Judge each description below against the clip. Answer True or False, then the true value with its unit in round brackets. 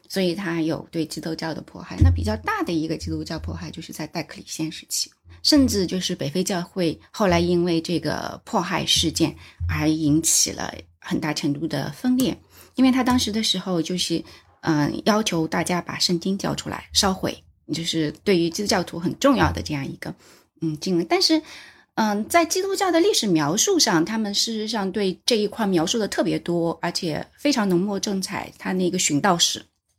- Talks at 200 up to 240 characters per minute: False (290 characters per minute)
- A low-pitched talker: False (175 Hz)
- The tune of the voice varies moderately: True (4.7 semitones)